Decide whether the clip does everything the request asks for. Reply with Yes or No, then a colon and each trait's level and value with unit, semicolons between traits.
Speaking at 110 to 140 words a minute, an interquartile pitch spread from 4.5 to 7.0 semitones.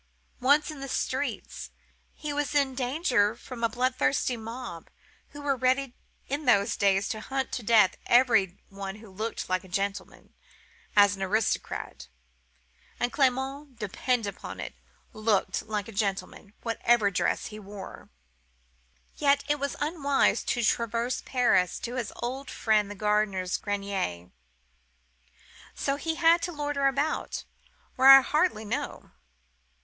Yes: slow, 135 wpm; average, 5.1 semitones